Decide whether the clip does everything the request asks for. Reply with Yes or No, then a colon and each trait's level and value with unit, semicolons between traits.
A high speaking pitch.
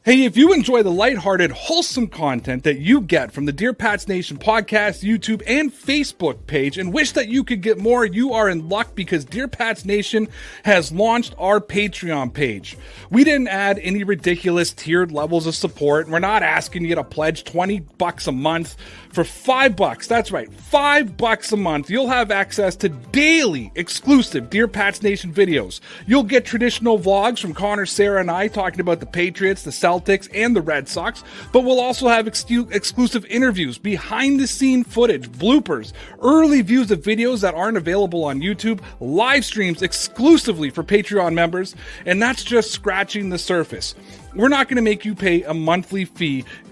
Yes: high, 205 Hz